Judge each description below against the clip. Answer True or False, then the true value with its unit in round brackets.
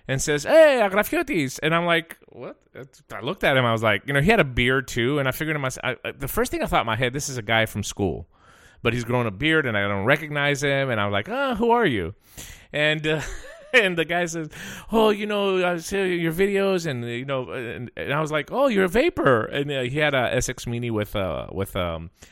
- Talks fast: True (260 wpm)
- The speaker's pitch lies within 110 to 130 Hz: False (140 Hz)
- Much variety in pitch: True (6.8 semitones)